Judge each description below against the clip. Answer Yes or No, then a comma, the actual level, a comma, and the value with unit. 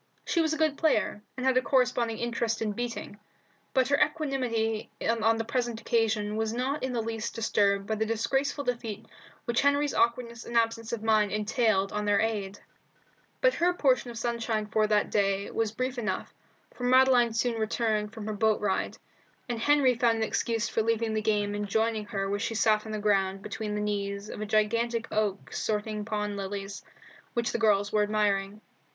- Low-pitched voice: No, high, 225 Hz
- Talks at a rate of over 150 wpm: Yes, average, 190 wpm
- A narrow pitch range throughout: Yes, narrow, 2.3 semitones